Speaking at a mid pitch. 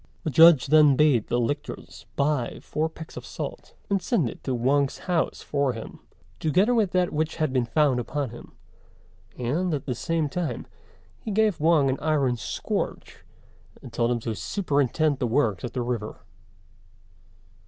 Yes: medium, 145 Hz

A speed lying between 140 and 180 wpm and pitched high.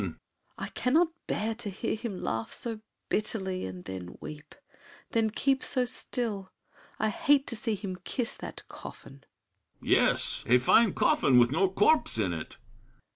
Yes: average, 150 wpm; high, 205 Hz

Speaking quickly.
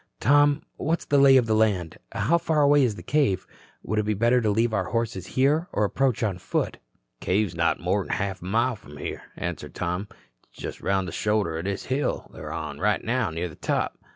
Yes: fast, 220 wpm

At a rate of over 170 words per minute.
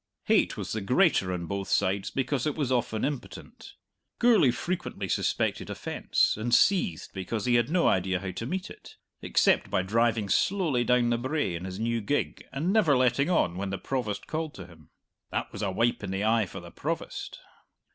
Yes: average, 195 wpm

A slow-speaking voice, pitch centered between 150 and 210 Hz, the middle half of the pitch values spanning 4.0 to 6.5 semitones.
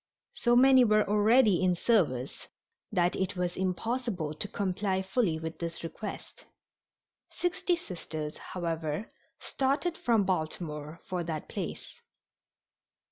Yes: slow, 115 wpm; medium, 185 Hz; wide, 5.5 semitones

